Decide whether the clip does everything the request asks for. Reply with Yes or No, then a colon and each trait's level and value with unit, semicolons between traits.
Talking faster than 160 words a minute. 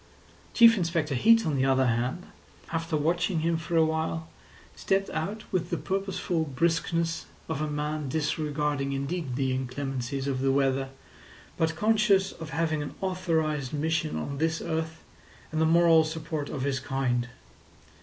No: average, 155 wpm